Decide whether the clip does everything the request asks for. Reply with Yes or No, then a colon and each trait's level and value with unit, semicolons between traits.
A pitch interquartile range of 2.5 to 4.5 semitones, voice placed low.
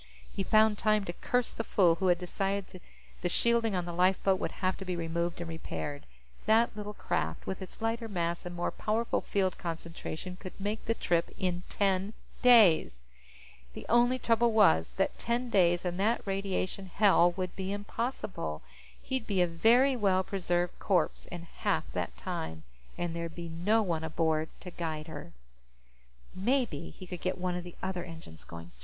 No: average, 3.7 semitones; medium, 185 Hz